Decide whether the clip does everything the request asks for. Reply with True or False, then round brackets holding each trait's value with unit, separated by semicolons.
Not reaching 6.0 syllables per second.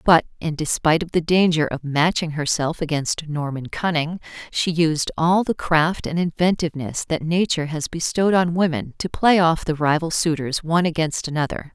True (5.1 syllables/s)